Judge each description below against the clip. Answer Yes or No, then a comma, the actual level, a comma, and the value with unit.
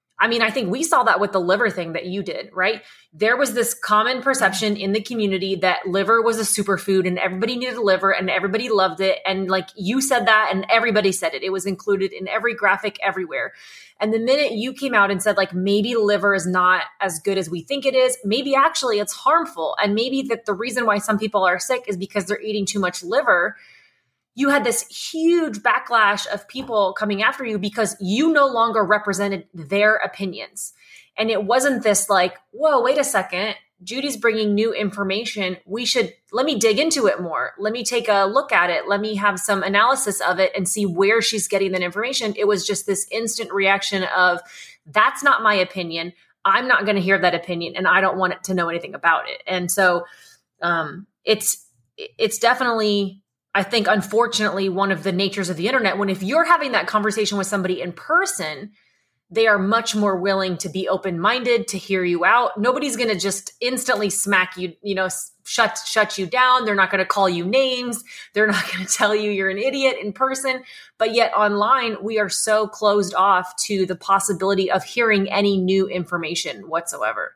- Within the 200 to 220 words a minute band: Yes, fast, 205 wpm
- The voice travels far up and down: No, average, 3.3 semitones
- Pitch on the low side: No, high, 205 Hz